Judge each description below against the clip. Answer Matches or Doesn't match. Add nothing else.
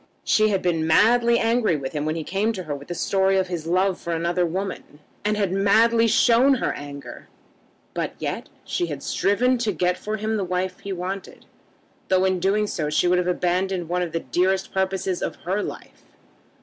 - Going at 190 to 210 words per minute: Matches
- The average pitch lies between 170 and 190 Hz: Matches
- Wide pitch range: Doesn't match